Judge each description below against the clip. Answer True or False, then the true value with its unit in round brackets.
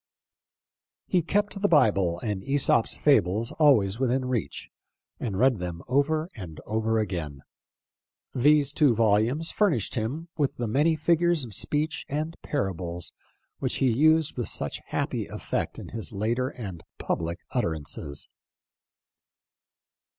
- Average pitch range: False (7.1 semitones)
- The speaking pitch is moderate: False (125 Hz)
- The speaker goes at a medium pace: False (130 wpm)